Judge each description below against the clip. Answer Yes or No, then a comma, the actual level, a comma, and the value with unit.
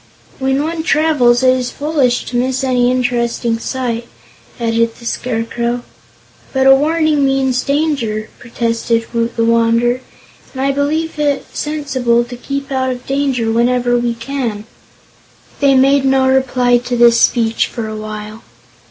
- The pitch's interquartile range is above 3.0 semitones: No, narrow, 2.5 semitones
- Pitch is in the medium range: No, very high, 250 Hz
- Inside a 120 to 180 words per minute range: Yes, average, 145 wpm